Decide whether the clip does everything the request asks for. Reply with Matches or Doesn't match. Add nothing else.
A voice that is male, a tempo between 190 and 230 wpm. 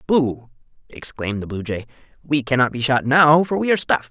Matches